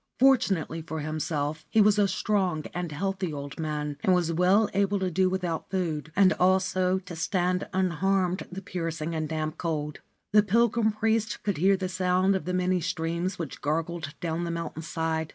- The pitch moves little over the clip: No, average, 3.1 semitones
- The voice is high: No, medium, 180 Hz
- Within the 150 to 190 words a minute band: Yes, average, 180 wpm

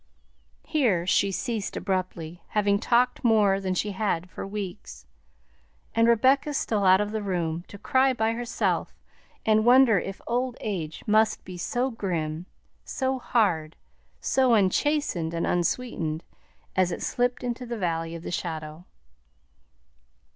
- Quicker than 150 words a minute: No, average, 140 wpm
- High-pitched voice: Yes, high, 205 Hz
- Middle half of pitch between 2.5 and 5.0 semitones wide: No, wide, 5.4 semitones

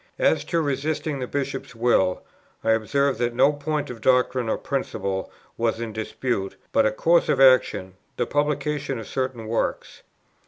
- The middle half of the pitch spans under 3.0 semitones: No, average, 4.0 semitones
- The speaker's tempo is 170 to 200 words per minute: No, average, 160 wpm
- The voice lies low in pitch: Yes, low, 130 Hz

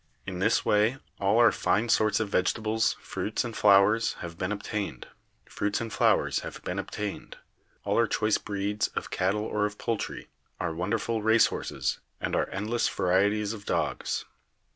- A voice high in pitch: No, low, 105 Hz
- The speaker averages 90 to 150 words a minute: Yes, average, 140 wpm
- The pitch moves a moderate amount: No, narrow, 2.0 semitones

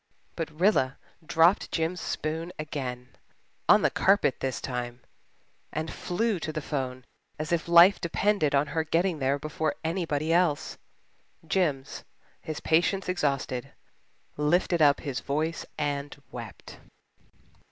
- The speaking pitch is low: No, medium, 155 Hz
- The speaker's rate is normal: No, slow, 125 wpm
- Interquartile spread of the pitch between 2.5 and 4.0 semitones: Yes, average, 3.5 semitones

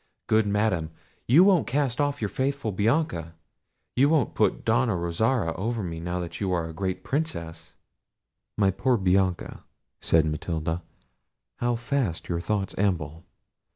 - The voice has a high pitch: No, low, 100 Hz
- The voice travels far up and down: Yes, wide, 6.4 semitones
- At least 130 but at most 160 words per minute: Yes, average, 140 wpm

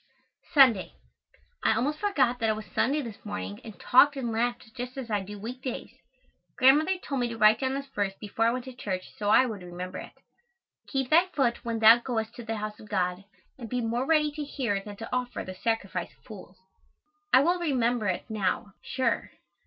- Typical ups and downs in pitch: Yes, average, 4.0 semitones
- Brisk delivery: Yes, fast, 210 wpm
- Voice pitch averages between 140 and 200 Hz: No, high, 235 Hz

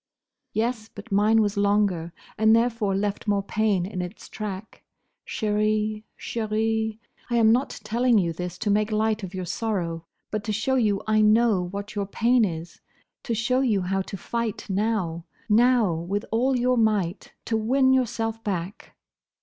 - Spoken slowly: No, average, 165 wpm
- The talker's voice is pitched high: Yes, high, 215 Hz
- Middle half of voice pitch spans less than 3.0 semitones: Yes, narrow, 2.4 semitones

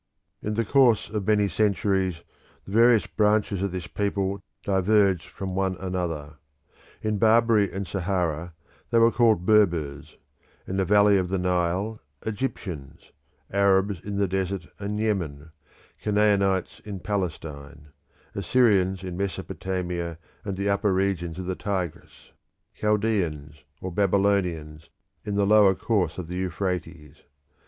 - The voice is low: Yes, very low, 95 Hz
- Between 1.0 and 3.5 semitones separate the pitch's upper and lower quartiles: Yes, average, 2.8 semitones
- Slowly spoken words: Yes, slow, 130 wpm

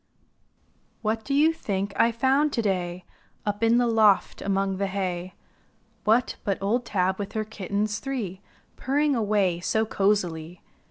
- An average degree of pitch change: Yes, average, 3.3 semitones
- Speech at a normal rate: Yes, average, 150 wpm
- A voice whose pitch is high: Yes, high, 205 Hz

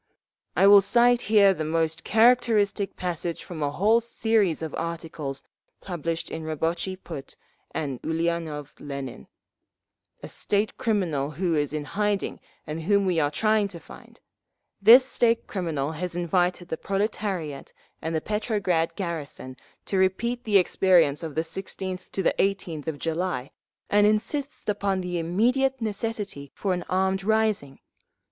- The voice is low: No, medium, 180 Hz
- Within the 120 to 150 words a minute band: Yes, average, 140 wpm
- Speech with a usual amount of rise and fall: Yes, average, 4.3 semitones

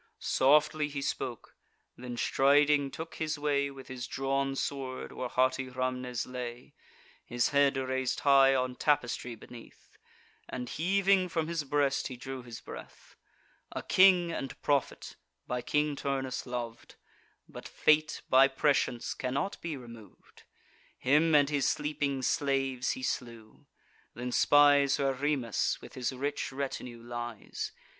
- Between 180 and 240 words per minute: No, slow, 135 wpm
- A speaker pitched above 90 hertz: Yes, low, 135 Hz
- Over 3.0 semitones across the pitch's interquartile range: No, narrow, 2.5 semitones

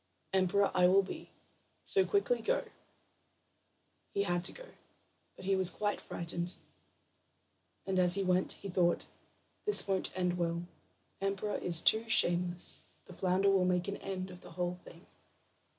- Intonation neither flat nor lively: No, narrow, 1.9 semitones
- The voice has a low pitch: No, medium, 185 Hz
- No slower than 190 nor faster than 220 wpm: No, average, 150 wpm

